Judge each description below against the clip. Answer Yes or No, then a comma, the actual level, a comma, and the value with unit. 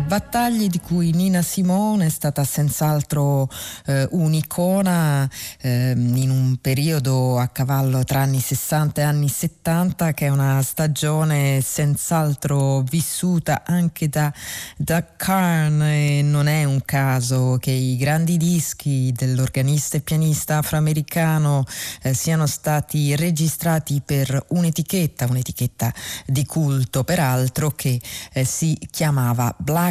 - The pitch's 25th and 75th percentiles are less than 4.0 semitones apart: Yes, average, 3.3 semitones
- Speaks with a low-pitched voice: No, medium, 145 Hz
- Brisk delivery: No, average, 120 wpm